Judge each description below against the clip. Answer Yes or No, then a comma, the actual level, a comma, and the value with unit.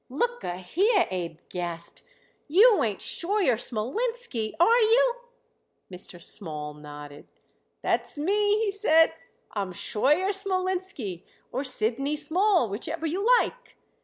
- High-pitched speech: Yes, very high, 300 Hz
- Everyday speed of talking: No, slow, 115 wpm